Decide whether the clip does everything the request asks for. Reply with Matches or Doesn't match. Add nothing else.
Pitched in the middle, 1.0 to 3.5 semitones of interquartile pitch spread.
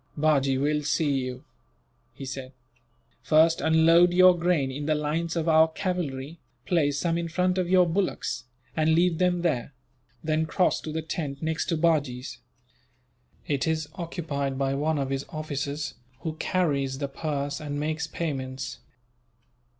Matches